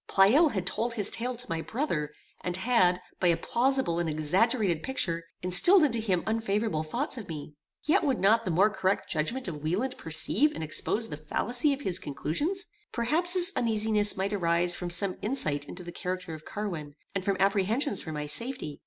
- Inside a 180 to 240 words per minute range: Yes, average, 190 wpm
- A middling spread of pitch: No, wide, 6.0 semitones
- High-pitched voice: Yes, high, 195 Hz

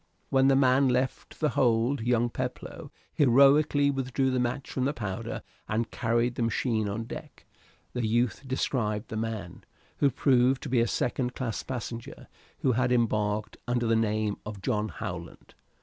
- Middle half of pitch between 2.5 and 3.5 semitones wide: Yes, average, 2.9 semitones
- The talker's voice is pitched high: No, low, 120 Hz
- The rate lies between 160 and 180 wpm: Yes, average, 165 wpm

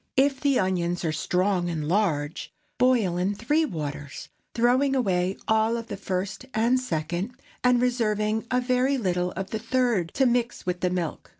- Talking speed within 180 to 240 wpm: No, average, 170 wpm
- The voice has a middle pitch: No, high, 210 Hz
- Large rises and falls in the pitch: Yes, wide, 5.7 semitones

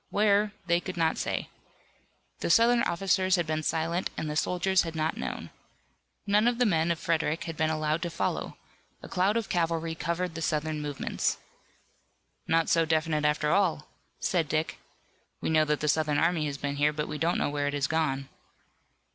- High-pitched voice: No, medium, 160 Hz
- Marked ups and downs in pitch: No, average, 2.7 semitones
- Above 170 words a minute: Yes, average, 190 wpm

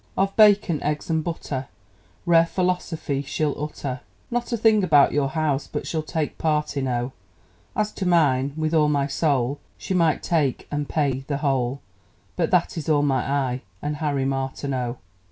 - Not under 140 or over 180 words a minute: Yes, average, 170 wpm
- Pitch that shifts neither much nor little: Yes, average, 3.3 semitones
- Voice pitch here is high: No, medium, 150 Hz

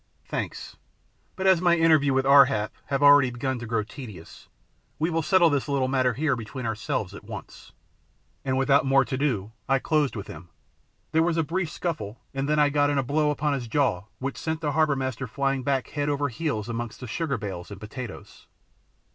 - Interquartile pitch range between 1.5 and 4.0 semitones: Yes, average, 3.7 semitones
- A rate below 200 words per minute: No, fast, 205 wpm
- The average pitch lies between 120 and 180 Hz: Yes, low, 135 Hz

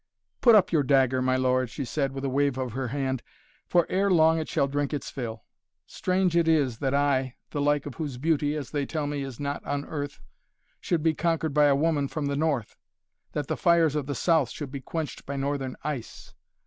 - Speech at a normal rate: No, fast, 220 wpm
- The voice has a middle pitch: Yes, medium, 145 Hz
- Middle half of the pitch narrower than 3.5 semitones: Yes, average, 2.8 semitones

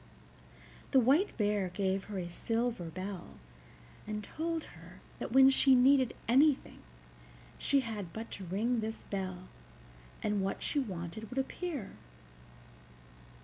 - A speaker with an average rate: No, slow, 130 wpm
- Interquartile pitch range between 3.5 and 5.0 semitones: No, wide, 5.6 semitones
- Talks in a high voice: Yes, high, 220 Hz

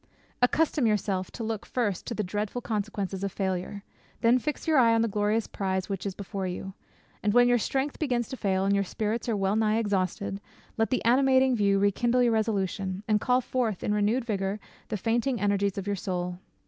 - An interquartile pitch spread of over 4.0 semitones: No, average, 3.3 semitones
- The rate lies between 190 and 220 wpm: Yes, average, 200 wpm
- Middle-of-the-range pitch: No, high, 210 Hz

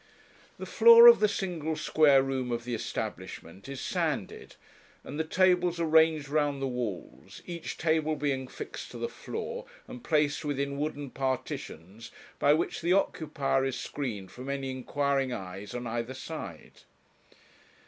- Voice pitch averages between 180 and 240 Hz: No, medium, 140 Hz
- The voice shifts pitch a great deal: No, average, 3.8 semitones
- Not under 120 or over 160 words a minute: Yes, average, 150 wpm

